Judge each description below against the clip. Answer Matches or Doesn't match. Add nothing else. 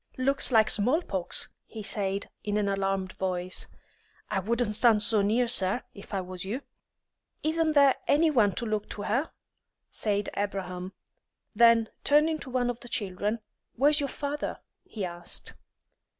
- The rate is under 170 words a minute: Matches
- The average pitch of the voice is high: Matches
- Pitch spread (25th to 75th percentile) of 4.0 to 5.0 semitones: Matches